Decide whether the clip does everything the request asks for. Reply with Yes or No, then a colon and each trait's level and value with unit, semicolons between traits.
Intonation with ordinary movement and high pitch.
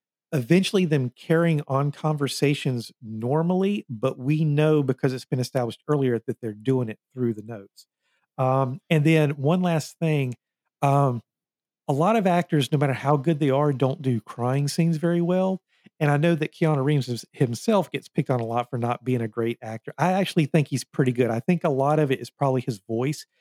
No: average, 4.1 semitones; medium, 140 Hz